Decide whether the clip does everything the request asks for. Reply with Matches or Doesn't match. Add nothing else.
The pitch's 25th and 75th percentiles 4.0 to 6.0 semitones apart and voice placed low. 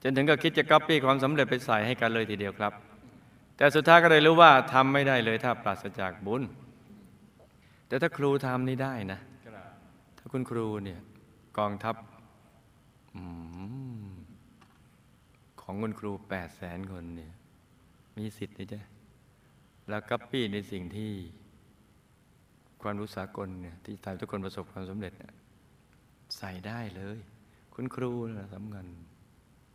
Matches